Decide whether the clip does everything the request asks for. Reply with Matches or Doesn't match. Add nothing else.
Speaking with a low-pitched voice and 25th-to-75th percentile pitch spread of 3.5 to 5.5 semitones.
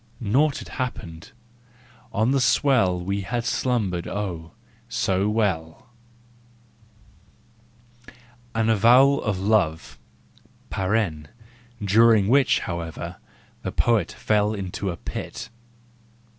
Matches